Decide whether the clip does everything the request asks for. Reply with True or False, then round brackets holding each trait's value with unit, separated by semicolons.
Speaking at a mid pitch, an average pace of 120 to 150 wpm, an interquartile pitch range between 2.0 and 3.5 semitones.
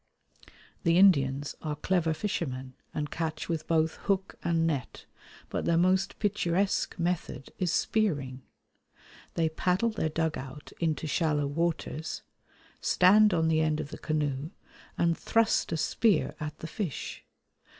True (160 Hz; 140 wpm; 3.2 semitones)